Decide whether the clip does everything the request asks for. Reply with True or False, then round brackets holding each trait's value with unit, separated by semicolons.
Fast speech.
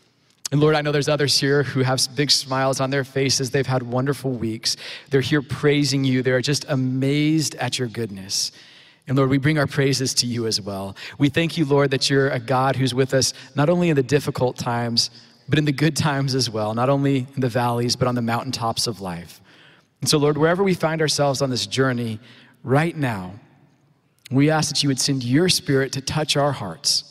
True (215 wpm)